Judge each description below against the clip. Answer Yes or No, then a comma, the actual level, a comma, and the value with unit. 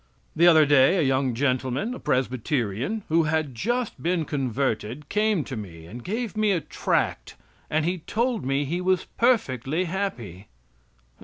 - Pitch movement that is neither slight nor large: No, wide, 6.5 semitones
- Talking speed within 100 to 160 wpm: Yes, average, 155 wpm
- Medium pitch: Yes, medium, 150 Hz